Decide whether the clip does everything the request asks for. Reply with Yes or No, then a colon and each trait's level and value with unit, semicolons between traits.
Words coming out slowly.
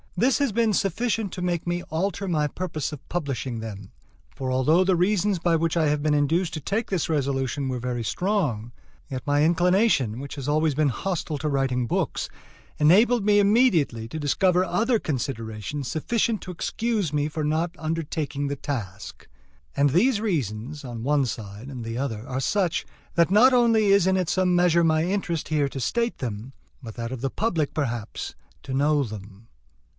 No: average, 180 wpm